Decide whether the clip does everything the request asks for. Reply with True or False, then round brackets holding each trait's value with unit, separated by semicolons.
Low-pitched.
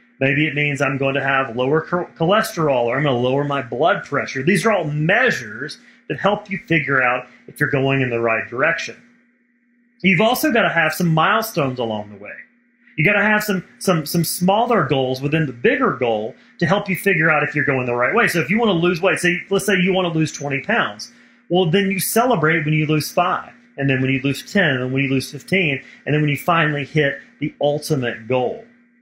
False (155 Hz)